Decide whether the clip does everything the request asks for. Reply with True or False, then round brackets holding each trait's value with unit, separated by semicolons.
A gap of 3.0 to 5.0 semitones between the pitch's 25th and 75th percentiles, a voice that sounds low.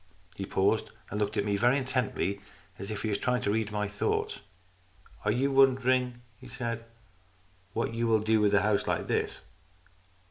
True (3.5 semitones; 110 Hz)